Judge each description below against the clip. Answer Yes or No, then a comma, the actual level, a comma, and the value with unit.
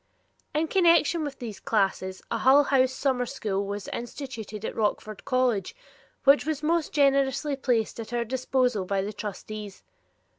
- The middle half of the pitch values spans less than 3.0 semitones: No, average, 4.6 semitones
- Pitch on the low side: No, very high, 250 Hz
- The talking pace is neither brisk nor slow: Yes, average, 150 wpm